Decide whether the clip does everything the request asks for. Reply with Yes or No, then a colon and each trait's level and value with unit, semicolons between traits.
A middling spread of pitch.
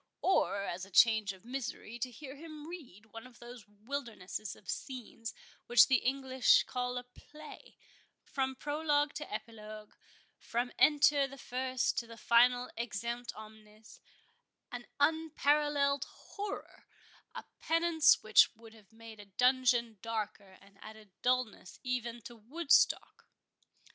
Yes: average, 4.3 semitones